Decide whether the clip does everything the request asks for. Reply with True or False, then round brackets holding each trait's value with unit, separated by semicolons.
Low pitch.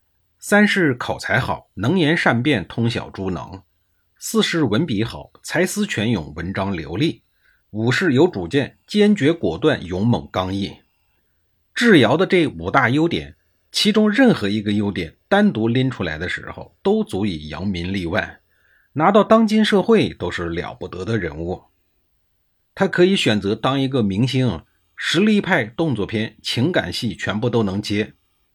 True (110 Hz)